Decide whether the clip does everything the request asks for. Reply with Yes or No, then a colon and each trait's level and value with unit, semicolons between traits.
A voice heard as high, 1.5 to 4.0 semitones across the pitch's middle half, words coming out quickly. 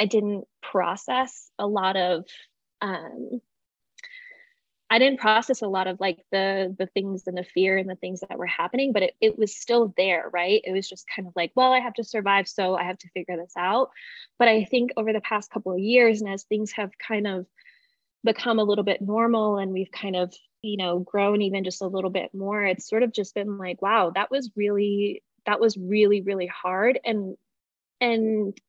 Yes: high, 205 Hz; average, 3.3 semitones; fast, 210 wpm